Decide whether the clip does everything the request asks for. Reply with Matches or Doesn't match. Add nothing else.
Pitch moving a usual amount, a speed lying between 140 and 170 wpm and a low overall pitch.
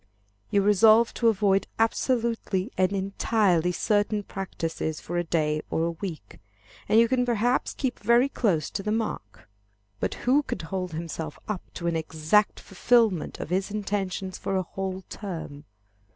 Doesn't match